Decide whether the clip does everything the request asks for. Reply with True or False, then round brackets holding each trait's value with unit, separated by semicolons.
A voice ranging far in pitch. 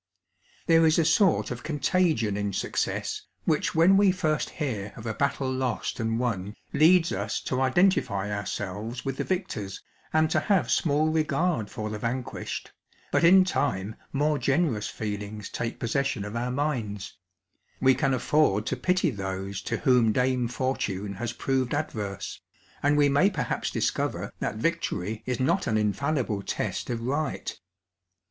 True (6.5 semitones)